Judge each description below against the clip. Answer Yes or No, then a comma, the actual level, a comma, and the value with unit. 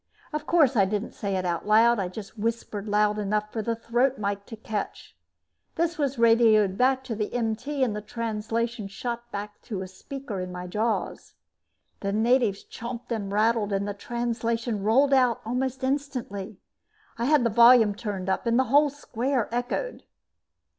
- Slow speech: No, average, 170 wpm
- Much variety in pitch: No, average, 3.2 semitones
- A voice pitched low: No, high, 230 Hz